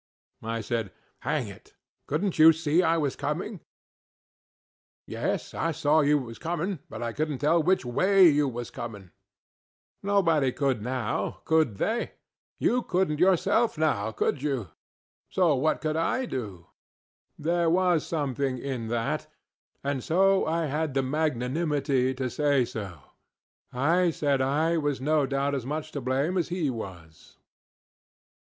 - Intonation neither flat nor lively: Yes, average, 4.5 semitones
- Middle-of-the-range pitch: Yes, medium, 145 Hz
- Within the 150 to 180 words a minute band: No, average, 140 wpm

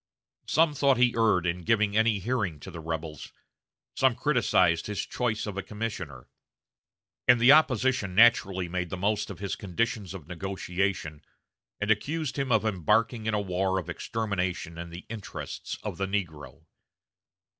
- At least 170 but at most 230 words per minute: No, average, 155 wpm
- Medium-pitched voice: No, low, 100 Hz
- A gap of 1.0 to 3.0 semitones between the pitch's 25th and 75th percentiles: No, average, 4.2 semitones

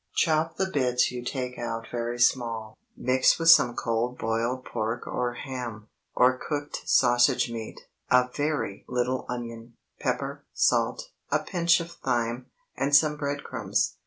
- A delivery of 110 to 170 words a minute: Yes, average, 145 wpm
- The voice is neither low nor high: No, low, 125 Hz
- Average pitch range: Yes, average, 3.3 semitones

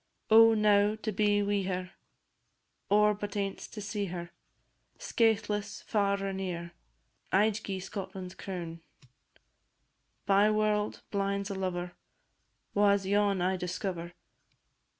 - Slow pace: Yes, slow, 125 wpm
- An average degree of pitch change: No, narrow, 1.9 semitones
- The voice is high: Yes, high, 200 Hz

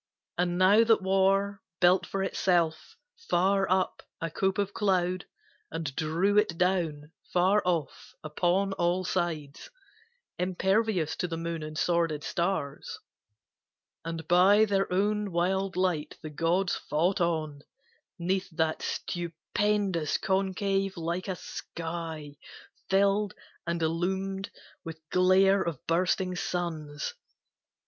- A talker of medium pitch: Yes, medium, 180 Hz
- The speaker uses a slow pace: Yes, slow, 115 wpm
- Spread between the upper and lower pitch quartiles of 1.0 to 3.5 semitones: Yes, average, 2.7 semitones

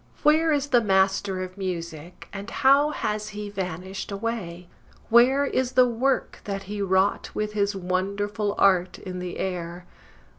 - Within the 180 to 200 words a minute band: No, average, 150 wpm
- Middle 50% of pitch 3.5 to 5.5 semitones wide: Yes, average, 3.8 semitones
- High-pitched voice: Yes, high, 200 Hz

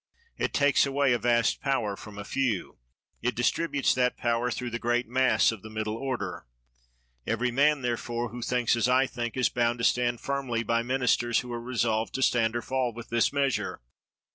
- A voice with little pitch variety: Yes, narrow, 1.7 semitones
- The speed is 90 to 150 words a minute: No, average, 190 wpm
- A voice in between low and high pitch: No, low, 120 Hz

